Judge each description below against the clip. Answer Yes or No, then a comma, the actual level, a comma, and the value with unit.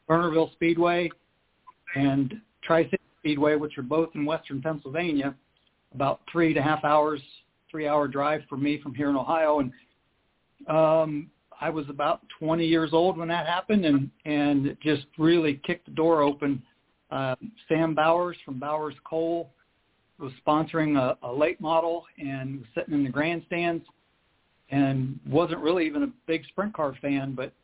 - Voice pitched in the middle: Yes, medium, 155 Hz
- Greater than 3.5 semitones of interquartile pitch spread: No, average, 2.7 semitones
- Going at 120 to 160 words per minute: Yes, average, 155 wpm